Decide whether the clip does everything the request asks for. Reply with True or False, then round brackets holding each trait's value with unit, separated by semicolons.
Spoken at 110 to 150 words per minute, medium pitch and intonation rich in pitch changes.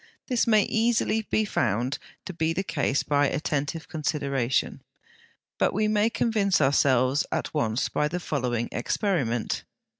True (140 wpm; 150 Hz; 7.5 semitones)